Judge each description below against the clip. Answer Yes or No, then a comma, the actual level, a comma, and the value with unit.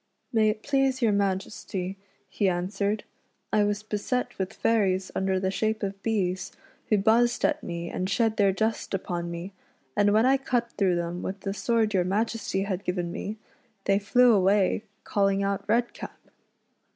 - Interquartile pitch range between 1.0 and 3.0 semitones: Yes, average, 2.7 semitones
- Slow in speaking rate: No, average, 175 wpm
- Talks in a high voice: Yes, high, 200 Hz